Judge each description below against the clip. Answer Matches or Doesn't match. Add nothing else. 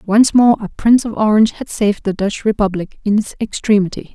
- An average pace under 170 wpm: Doesn't match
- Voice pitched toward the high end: Matches